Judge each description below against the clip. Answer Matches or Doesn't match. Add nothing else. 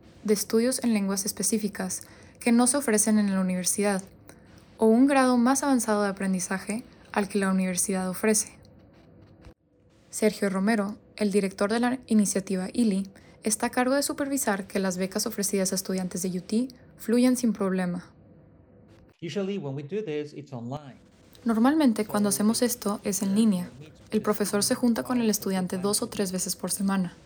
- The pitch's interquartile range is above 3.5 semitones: Doesn't match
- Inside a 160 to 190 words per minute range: Doesn't match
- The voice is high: Matches